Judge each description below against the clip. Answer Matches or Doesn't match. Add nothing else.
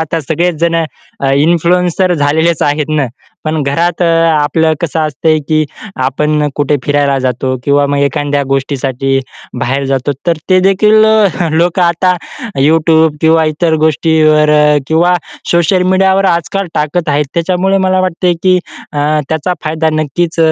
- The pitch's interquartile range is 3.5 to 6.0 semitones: Doesn't match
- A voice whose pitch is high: Doesn't match